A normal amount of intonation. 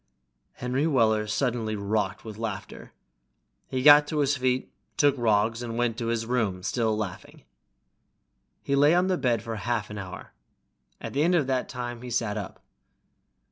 Yes: average, 3.4 semitones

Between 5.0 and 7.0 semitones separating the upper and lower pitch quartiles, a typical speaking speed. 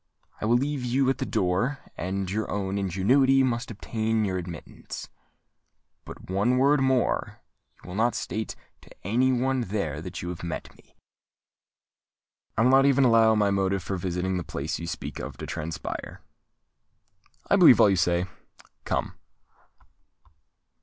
Yes: wide, 5.5 semitones; average, 155 wpm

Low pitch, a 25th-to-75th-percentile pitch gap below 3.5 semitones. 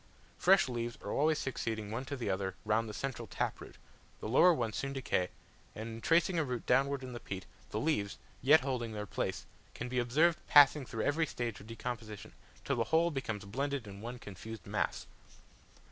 No: low, 120 Hz; average, 4.3 semitones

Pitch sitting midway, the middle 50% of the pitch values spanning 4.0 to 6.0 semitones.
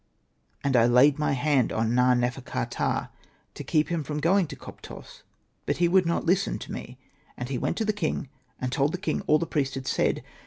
Yes: medium, 145 Hz; average, 5.0 semitones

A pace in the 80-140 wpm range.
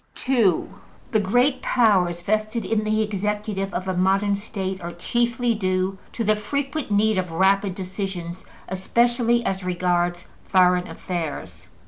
Yes: slow, 135 wpm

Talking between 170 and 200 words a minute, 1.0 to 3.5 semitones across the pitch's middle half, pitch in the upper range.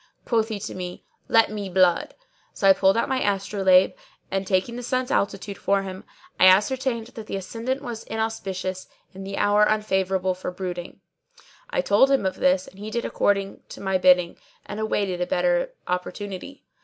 Yes: average, 180 wpm; average, 3.1 semitones; high, 200 Hz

